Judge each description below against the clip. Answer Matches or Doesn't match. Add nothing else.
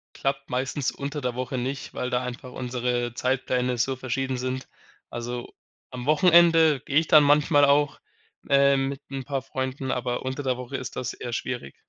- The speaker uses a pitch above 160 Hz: Doesn't match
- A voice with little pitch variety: Matches